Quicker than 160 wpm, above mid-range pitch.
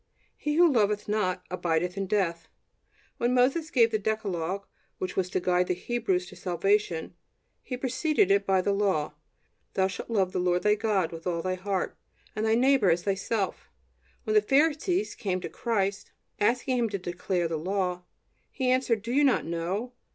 Yes: average, 180 wpm; high, 200 Hz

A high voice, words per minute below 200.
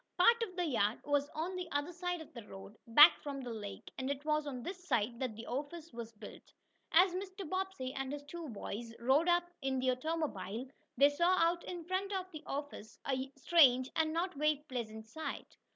No: very high, 290 Hz; fast, 205 wpm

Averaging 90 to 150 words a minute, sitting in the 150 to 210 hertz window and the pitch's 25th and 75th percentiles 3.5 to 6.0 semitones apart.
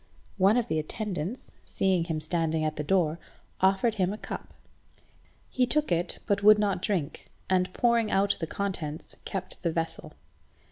No: average, 160 wpm; high, 190 Hz; average, 4.2 semitones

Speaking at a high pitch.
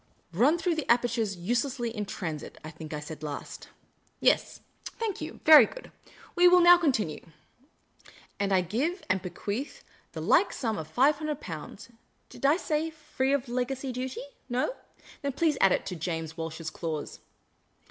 Yes: high, 240 Hz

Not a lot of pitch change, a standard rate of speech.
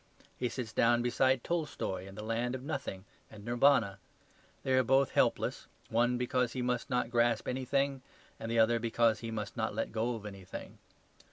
Yes: narrow, 2.3 semitones; average, 180 wpm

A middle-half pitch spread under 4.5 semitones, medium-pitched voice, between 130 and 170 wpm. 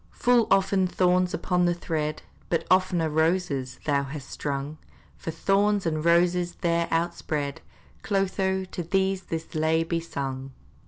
Yes: average, 3.2 semitones; medium, 170 Hz; average, 140 wpm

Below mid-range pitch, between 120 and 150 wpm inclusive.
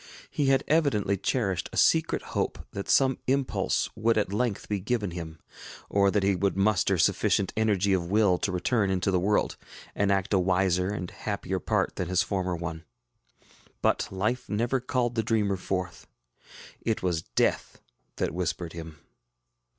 No: low, 100 Hz; average, 165 wpm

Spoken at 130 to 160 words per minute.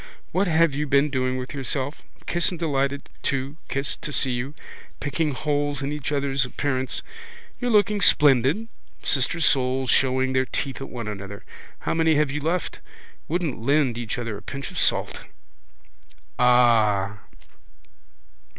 Yes: average, 150 wpm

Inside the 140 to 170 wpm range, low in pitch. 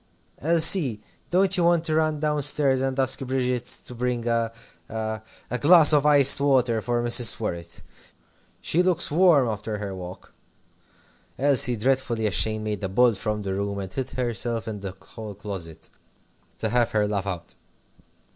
Yes: average, 165 wpm; low, 120 Hz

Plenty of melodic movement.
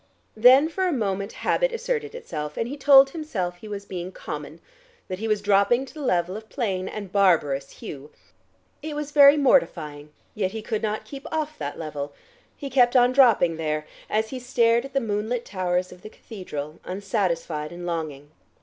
Yes: wide, 7.1 semitones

